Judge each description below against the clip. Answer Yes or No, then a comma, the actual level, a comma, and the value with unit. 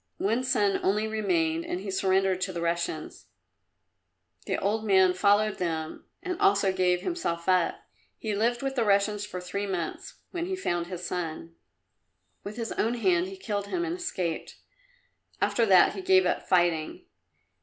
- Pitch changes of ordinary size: Yes, average, 3.5 semitones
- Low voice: No, high, 195 Hz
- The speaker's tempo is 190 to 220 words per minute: No, average, 165 wpm